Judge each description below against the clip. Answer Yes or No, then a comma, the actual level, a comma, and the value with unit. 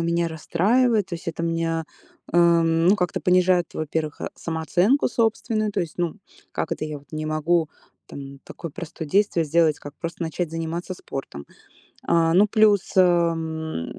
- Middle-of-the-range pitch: Yes, medium, 170 Hz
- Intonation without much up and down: Yes, narrow, 2.1 semitones